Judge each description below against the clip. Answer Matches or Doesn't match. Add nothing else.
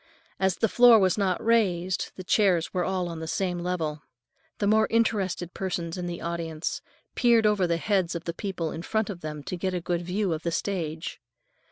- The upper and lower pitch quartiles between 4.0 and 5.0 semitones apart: Doesn't match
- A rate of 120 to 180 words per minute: Doesn't match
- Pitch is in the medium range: Matches